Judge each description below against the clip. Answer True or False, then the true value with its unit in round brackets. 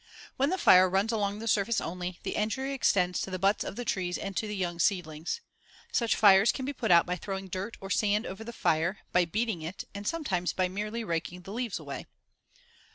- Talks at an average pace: False (220 wpm)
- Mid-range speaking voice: False (195 Hz)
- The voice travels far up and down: False (3.7 semitones)